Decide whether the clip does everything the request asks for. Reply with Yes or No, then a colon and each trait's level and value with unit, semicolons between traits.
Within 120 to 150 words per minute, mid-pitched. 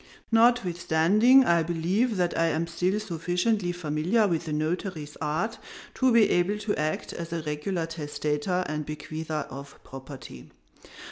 Yes: average, 140 wpm; medium, 170 Hz